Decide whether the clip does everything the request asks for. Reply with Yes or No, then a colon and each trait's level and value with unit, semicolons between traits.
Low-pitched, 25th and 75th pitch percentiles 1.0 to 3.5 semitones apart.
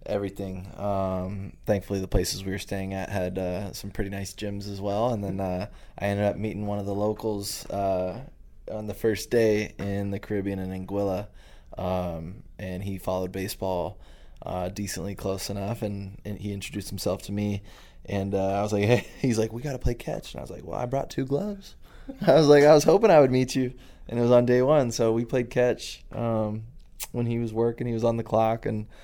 Yes: low, 100 Hz; average, 3.2 semitones